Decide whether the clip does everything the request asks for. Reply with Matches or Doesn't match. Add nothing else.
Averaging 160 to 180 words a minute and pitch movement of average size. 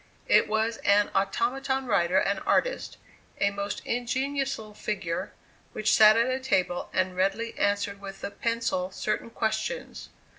Doesn't match